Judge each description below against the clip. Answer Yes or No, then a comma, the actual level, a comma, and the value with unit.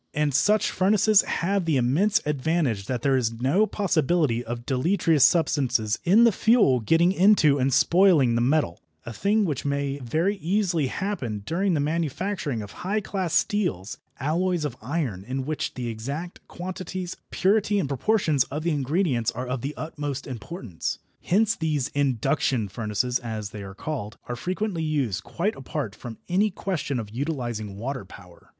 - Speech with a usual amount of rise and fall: No, wide, 6.9 semitones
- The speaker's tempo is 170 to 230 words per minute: No, average, 160 wpm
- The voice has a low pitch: No, medium, 145 Hz